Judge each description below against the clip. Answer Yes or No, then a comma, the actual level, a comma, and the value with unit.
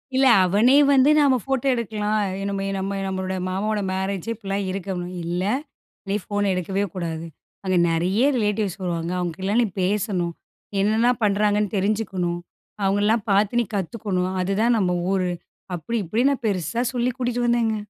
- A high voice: Yes, high, 200 Hz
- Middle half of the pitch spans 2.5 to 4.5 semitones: Yes, average, 3.3 semitones